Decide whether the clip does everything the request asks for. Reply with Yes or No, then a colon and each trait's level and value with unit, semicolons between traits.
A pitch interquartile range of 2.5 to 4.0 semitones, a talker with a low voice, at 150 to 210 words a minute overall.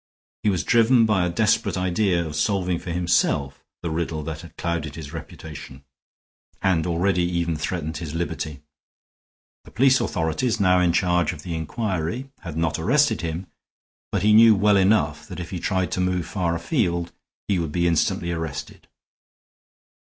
Yes: average, 3.3 semitones; very low, 85 Hz; average, 165 wpm